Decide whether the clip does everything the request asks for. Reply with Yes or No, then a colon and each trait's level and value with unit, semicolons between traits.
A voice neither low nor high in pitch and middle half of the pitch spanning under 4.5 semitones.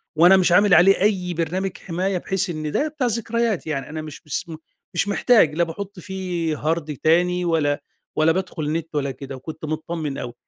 Yes: medium, 170 Hz; average, 3.6 semitones